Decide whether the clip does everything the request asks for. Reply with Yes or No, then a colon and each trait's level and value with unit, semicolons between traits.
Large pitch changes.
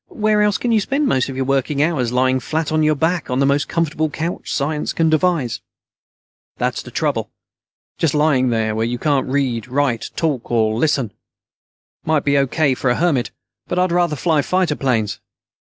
No: average, 4.1 semitones